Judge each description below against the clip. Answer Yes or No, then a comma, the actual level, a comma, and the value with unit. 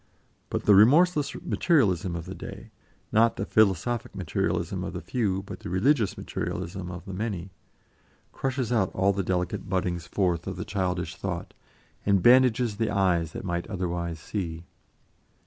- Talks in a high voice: No, very low, 95 Hz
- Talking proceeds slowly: No, average, 155 wpm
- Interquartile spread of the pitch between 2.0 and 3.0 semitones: No, average, 3.8 semitones